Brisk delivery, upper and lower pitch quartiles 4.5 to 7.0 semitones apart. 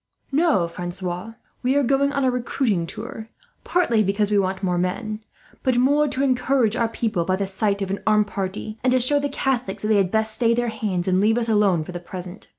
Yes: fast, 220 wpm; average, 4.8 semitones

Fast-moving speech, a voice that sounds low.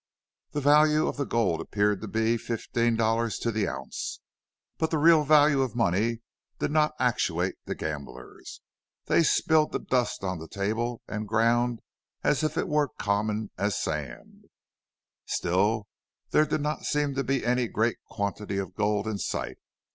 No: average, 165 wpm; low, 115 Hz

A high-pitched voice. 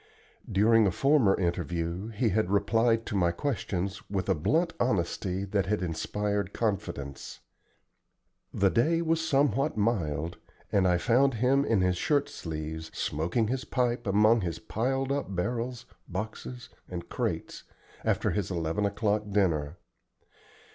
No: low, 105 Hz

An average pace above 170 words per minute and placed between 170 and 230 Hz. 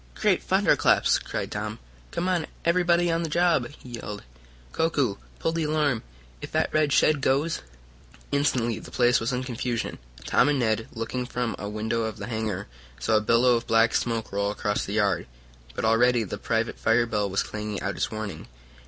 No: average, 190 wpm; low, 115 Hz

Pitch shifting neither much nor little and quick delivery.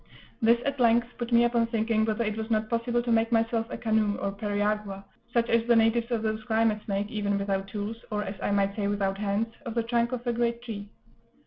No: narrow, 2.3 semitones; fast, 230 wpm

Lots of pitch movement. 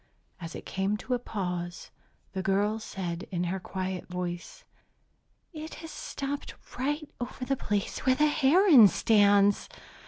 Yes: wide, 6.3 semitones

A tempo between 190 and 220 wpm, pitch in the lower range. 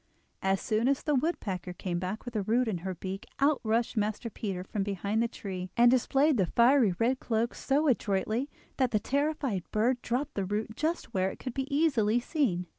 No: average, 200 wpm; high, 225 Hz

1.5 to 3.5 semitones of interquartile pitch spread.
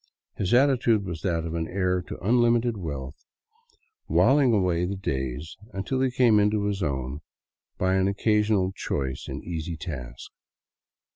No: average, 5.0 semitones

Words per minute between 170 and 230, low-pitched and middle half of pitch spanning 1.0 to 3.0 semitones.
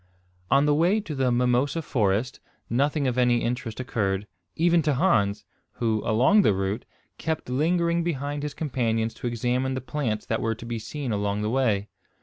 No: average, 175 wpm; low, 125 Hz; average, 4.7 semitones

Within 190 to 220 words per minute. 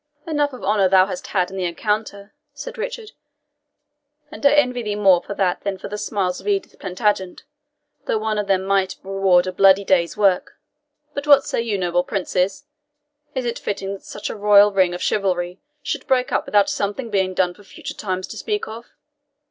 Yes: average, 195 wpm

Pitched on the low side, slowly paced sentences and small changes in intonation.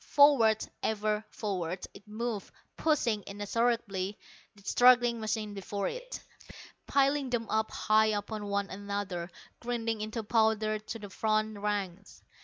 No: high, 215 Hz; slow, 120 wpm; narrow, 2.3 semitones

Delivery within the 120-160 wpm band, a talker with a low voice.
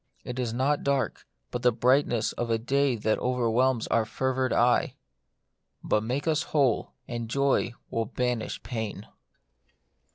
Yes: average, 150 wpm; low, 125 Hz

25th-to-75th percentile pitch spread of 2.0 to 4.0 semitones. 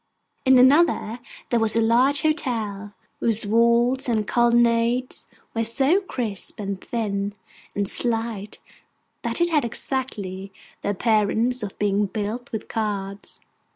Yes: average, 3.3 semitones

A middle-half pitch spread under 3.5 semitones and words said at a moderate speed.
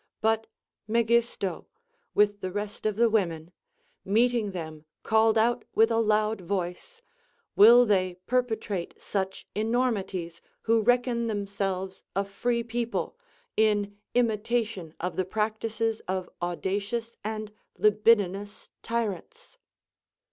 No: average, 2.9 semitones; slow, 110 wpm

